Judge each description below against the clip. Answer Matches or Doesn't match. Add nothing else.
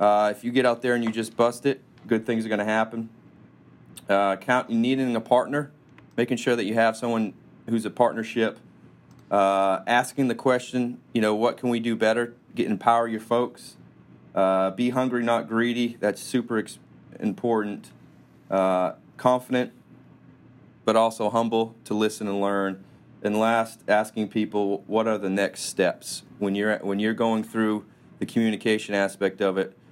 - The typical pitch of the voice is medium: Doesn't match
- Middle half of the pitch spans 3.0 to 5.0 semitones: Doesn't match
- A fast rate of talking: Doesn't match